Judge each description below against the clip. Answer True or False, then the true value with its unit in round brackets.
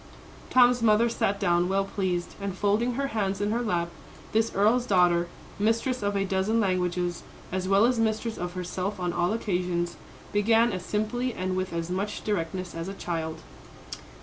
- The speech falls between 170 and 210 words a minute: True (175 wpm)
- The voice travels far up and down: False (3.6 semitones)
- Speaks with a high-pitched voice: True (195 Hz)